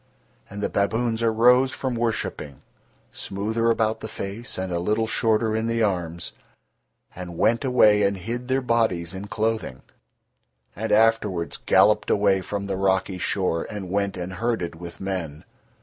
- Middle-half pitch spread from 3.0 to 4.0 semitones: Yes, average, 3.4 semitones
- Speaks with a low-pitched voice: Yes, low, 105 Hz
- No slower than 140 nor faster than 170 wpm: Yes, average, 150 wpm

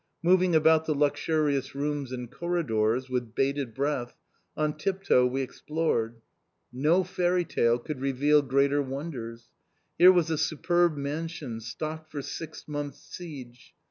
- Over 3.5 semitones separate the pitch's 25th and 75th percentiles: Yes, average, 3.9 semitones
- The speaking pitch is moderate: Yes, medium, 145 Hz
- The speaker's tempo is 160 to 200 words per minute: No, average, 140 wpm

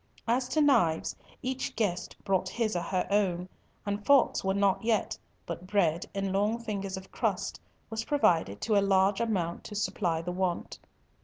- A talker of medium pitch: No, high, 195 Hz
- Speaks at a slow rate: No, average, 170 wpm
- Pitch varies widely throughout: No, average, 3.4 semitones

